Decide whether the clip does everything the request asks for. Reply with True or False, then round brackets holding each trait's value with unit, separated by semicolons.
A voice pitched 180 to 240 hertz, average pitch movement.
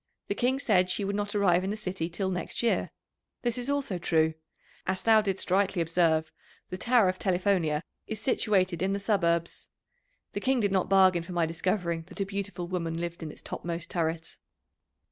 True (185 Hz; 3.0 semitones)